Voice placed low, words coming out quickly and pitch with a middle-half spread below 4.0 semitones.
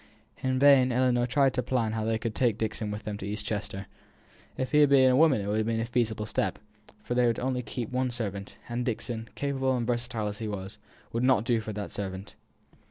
Yes: low, 115 Hz; fast, 235 wpm; average, 3.1 semitones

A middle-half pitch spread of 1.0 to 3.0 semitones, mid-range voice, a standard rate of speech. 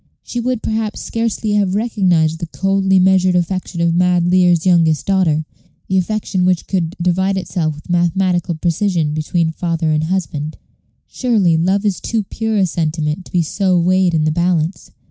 Yes: average, 2.7 semitones; medium, 180 Hz; average, 165 wpm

